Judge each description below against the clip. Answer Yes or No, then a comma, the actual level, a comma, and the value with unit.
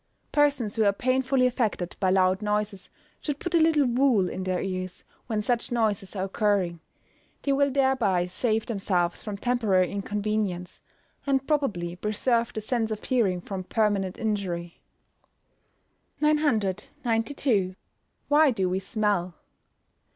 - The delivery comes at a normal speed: No, slow, 130 wpm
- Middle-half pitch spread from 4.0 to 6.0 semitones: Yes, average, 5.0 semitones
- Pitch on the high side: Yes, high, 210 Hz